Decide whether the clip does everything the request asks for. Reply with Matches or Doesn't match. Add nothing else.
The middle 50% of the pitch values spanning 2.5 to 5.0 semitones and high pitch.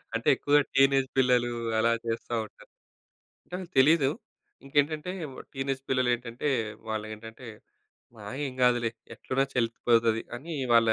Doesn't match